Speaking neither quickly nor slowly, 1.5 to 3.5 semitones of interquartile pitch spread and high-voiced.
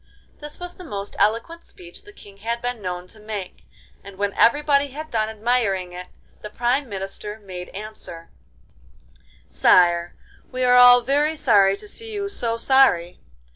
No: average, 160 wpm; wide, 5.6 semitones; high, 220 Hz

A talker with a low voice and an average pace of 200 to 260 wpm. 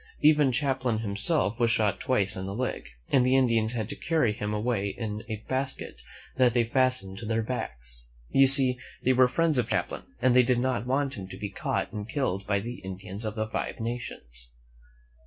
Yes: low, 115 Hz; fast, 205 wpm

